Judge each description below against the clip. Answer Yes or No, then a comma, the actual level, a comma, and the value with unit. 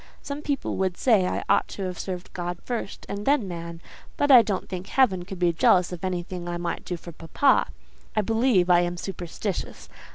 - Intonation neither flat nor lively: Yes, average, 3.2 semitones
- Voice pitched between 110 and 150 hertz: No, medium, 185 Hz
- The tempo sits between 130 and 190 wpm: No, average, 200 wpm